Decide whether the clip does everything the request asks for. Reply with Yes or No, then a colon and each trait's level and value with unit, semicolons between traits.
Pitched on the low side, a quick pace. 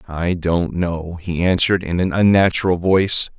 No: very low, 90 Hz; average, 160 wpm